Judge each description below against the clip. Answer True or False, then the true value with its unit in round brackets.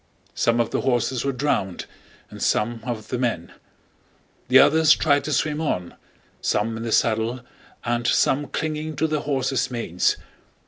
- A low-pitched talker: True (125 Hz)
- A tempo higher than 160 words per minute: False (155 wpm)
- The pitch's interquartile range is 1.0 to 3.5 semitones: False (4.3 semitones)